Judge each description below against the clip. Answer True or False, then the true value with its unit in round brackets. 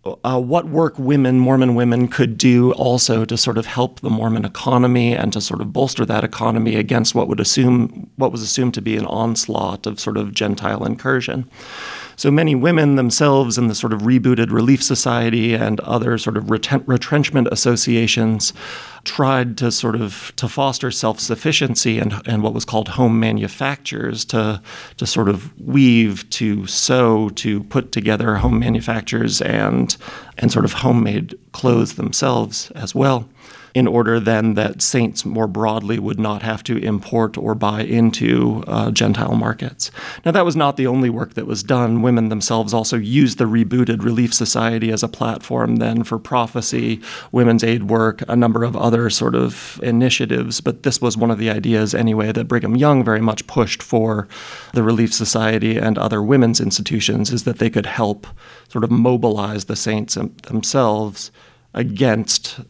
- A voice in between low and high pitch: False (115 Hz)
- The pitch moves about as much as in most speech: False (2.3 semitones)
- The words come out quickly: False (170 wpm)